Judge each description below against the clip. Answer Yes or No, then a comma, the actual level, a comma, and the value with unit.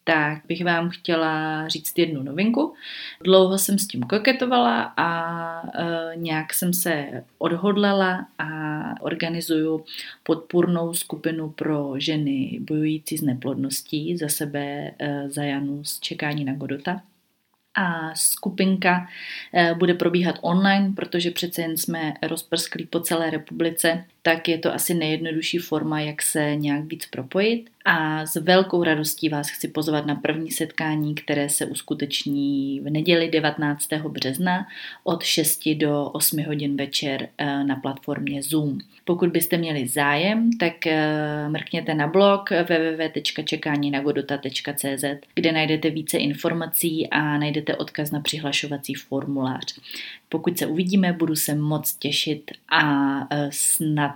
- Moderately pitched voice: Yes, medium, 155 Hz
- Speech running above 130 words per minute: No, average, 125 wpm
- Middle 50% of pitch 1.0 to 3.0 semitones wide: Yes, narrow, 2.6 semitones